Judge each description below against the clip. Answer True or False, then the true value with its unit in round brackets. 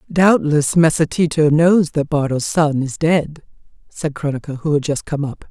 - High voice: False (155 Hz)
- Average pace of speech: True (175 wpm)